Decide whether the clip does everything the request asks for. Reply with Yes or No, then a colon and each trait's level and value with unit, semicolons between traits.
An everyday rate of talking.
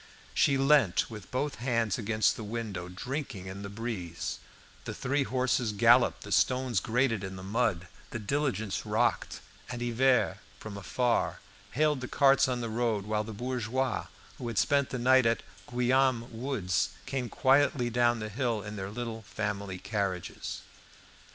Yes: average, 160 wpm